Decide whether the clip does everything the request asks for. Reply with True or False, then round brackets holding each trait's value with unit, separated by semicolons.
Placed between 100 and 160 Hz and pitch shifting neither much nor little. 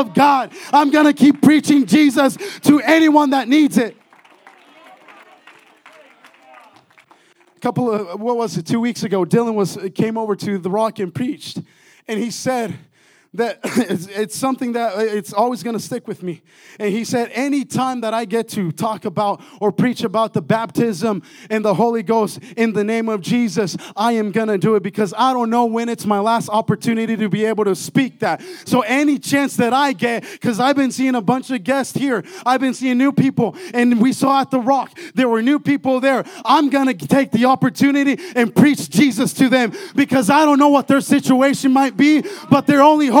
False (240 Hz; 3.9 semitones)